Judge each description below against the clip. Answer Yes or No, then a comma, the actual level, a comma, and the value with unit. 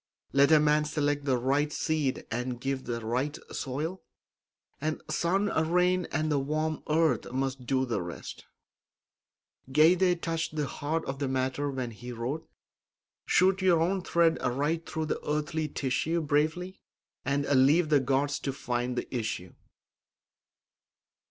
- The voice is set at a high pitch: No, medium, 145 Hz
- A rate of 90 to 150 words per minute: Yes, average, 145 wpm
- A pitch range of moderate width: Yes, average, 3.3 semitones